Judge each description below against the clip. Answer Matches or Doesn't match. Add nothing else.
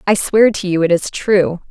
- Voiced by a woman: Matches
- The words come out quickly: Matches